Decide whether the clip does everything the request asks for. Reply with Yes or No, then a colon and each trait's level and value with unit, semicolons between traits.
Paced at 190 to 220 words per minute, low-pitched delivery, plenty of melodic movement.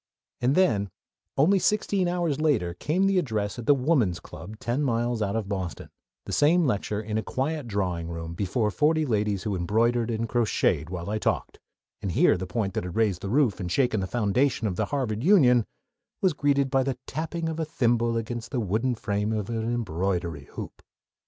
Yes: average, 195 wpm; low, 115 Hz; wide, 5.7 semitones